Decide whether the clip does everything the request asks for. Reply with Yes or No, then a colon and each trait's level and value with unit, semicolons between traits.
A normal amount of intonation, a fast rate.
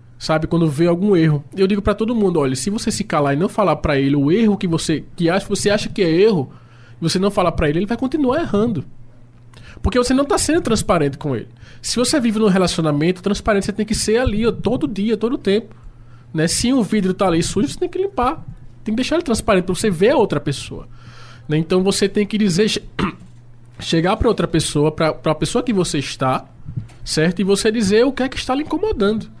No: wide, 6.8 semitones; fast, 235 wpm